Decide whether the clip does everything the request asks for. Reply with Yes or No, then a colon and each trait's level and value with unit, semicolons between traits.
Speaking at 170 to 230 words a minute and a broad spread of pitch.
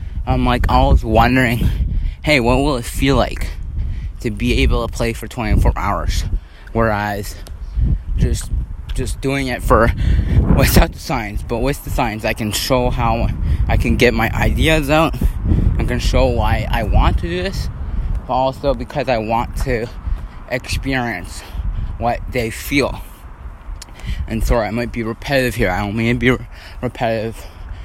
No: average, 160 wpm; wide, 5.9 semitones